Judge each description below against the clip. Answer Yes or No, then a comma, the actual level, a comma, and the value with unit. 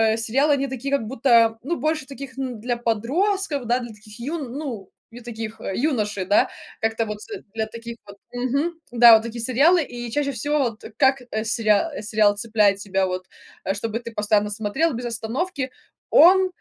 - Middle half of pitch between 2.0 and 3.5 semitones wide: No, average, 4.1 semitones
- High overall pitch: Yes, high, 235 Hz